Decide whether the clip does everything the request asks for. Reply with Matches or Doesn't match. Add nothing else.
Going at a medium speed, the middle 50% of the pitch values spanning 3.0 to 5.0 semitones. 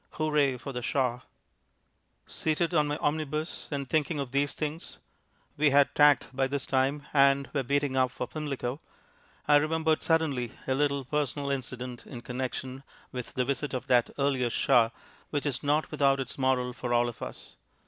Doesn't match